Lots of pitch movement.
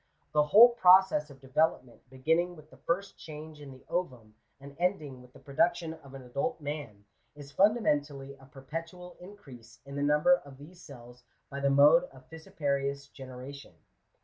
No: average, 3.8 semitones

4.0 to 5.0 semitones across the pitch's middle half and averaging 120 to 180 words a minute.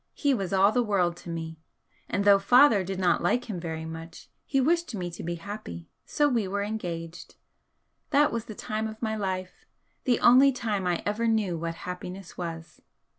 No: average, 4.6 semitones; average, 190 wpm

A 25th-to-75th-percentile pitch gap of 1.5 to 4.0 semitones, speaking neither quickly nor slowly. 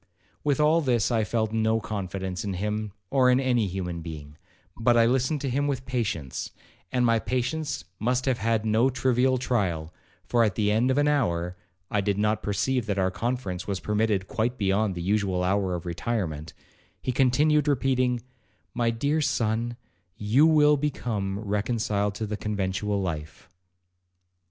No: average, 4.4 semitones; average, 165 wpm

